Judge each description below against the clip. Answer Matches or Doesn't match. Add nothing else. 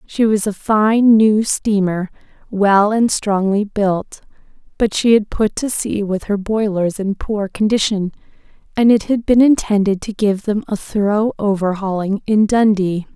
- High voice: Matches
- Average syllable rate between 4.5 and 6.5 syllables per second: Doesn't match